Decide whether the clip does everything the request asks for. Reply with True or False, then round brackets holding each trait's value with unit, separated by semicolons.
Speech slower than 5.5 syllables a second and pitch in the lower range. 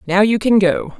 False (4.8 syllables/s; 205 Hz)